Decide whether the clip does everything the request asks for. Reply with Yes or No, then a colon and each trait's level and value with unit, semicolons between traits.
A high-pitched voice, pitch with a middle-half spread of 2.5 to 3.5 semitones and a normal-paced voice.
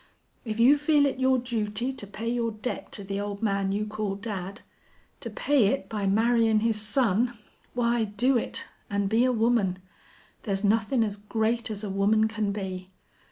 Yes: high, 220 Hz; average, 2.9 semitones; average, 180 wpm